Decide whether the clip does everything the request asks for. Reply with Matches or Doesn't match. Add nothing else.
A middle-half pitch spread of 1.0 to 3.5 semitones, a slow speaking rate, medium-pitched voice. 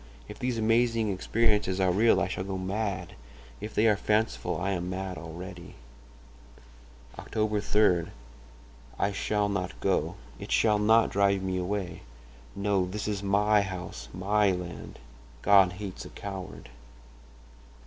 Doesn't match